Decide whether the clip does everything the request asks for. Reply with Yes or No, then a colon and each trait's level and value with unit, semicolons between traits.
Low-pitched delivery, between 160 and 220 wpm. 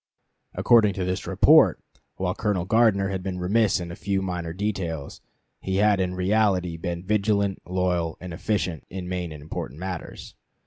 Yes: very low, 95 Hz; average, 165 wpm